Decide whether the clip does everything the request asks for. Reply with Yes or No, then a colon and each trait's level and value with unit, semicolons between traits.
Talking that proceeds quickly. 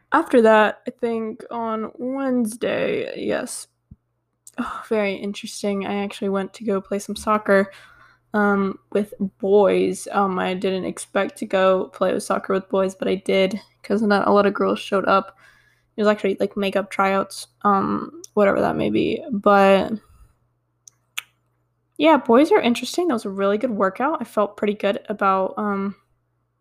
No: average, 160 wpm